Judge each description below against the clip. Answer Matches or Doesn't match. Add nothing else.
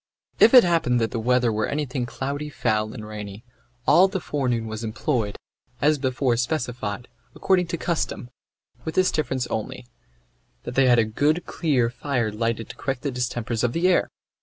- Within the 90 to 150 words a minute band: Doesn't match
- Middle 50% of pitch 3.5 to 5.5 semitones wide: Matches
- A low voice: Matches